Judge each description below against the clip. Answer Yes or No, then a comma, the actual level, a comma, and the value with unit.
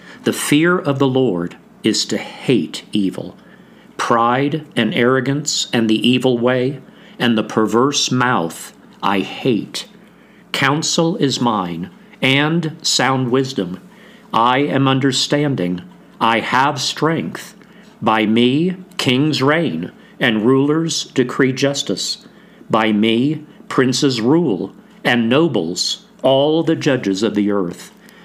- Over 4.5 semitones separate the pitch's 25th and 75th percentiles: No, average, 4.2 semitones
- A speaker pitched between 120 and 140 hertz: Yes, low, 135 Hz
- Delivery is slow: Yes, slow, 115 wpm